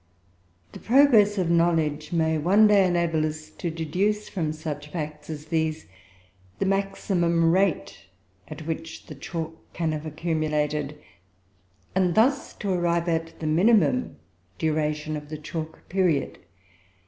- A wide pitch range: No, average, 3.0 semitones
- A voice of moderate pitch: Yes, medium, 160 Hz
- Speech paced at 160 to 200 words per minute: No, slow, 135 wpm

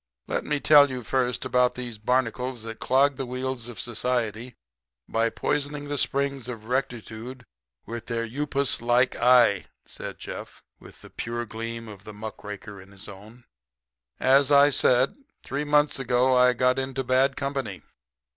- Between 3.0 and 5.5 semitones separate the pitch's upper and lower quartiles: No, narrow, 2.6 semitones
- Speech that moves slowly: No, average, 160 wpm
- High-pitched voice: No, low, 125 Hz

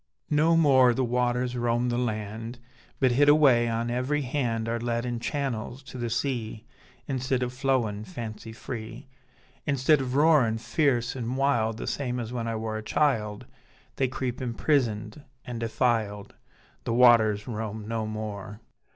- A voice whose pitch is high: No, low, 120 Hz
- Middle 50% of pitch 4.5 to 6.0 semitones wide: No, average, 2.8 semitones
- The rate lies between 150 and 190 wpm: Yes, average, 155 wpm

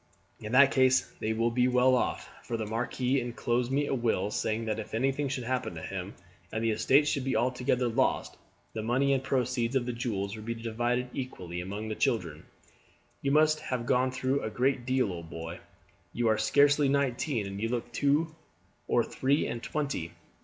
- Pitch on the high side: No, low, 120 Hz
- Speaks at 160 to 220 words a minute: Yes, average, 195 wpm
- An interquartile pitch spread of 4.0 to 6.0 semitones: No, average, 3.2 semitones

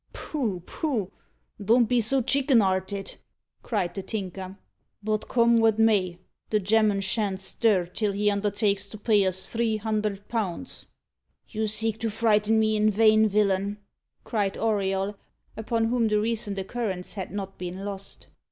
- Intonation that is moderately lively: No, narrow, 2.3 semitones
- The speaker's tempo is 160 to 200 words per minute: No, average, 150 wpm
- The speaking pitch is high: Yes, high, 210 Hz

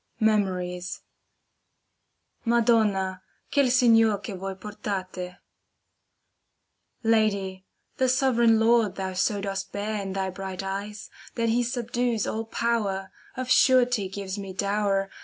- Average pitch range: Yes, average, 3.1 semitones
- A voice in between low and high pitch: No, high, 205 Hz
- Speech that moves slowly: Yes, slow, 120 wpm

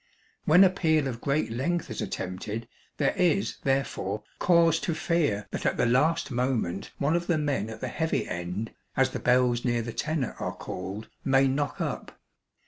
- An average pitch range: No, wide, 6.2 semitones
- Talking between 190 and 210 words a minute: No, average, 180 wpm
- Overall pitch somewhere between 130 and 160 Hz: Yes, low, 135 Hz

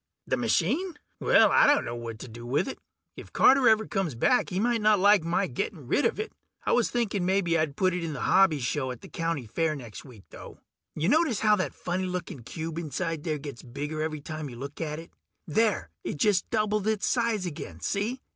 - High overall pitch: No, medium, 170 Hz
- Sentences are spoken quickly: Yes, fast, 220 wpm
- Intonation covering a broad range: Yes, wide, 6.6 semitones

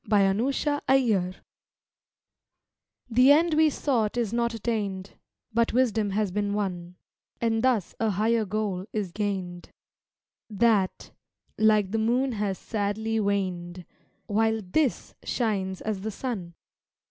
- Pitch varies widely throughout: No, average, 3.2 semitones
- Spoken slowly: Yes, slow, 125 wpm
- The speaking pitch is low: No, high, 215 Hz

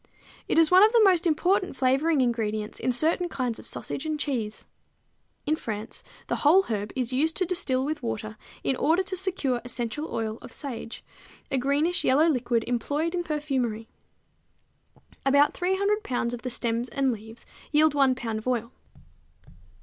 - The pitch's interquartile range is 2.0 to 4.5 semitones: No, wide, 5.4 semitones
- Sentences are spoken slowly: No, average, 165 wpm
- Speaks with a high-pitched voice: Yes, very high, 270 Hz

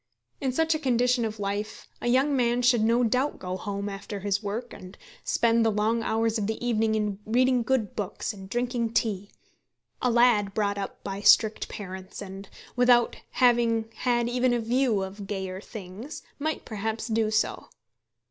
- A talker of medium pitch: No, high, 225 Hz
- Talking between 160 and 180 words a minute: Yes, average, 175 wpm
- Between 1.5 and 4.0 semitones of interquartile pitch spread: Yes, average, 3.1 semitones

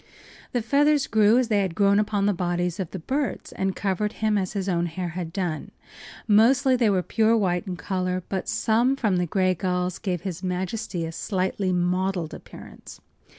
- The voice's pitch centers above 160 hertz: Yes, high, 190 Hz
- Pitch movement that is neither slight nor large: Yes, average, 3.2 semitones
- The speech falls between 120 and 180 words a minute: No, average, 190 wpm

